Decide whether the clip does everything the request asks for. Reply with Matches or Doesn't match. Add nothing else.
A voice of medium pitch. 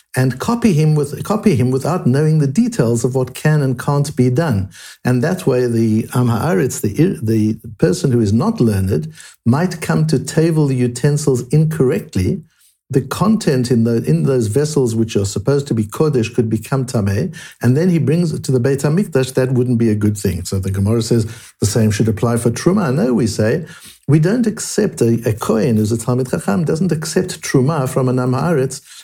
Doesn't match